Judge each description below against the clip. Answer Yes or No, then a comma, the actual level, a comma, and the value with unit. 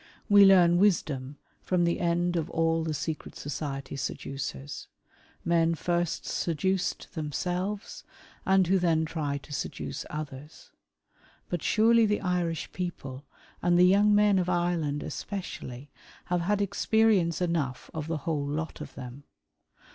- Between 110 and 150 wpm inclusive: Yes, average, 140 wpm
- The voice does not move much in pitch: No, average, 3.8 semitones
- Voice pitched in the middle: Yes, medium, 170 Hz